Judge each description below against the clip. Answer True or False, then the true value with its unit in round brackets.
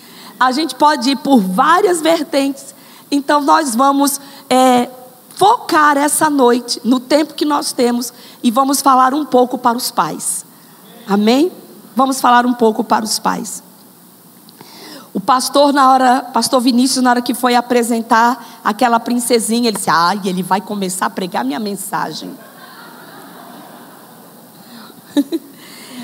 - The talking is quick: False (135 wpm)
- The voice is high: True (250 Hz)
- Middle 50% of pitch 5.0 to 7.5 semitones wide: False (3.1 semitones)